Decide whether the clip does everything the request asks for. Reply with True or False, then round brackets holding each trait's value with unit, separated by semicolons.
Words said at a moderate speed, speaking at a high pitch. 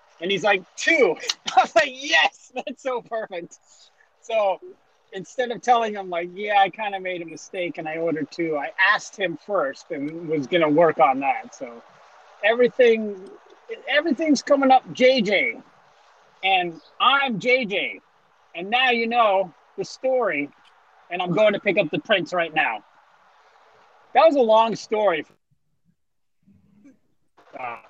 True (150 wpm; 210 Hz)